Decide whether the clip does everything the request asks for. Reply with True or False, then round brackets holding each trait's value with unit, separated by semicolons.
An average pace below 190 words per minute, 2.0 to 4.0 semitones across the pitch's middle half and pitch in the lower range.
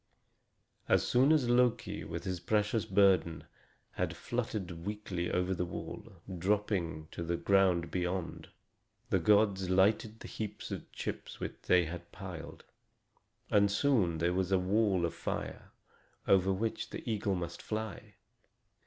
True (140 wpm; 3.3 semitones; 95 Hz)